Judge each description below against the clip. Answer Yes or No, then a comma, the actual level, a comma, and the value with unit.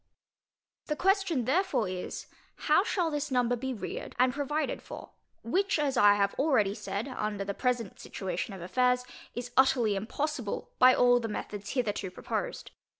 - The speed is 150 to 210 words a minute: Yes, average, 155 wpm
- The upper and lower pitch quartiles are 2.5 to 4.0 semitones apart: No, average, 5.2 semitones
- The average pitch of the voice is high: Yes, high, 245 Hz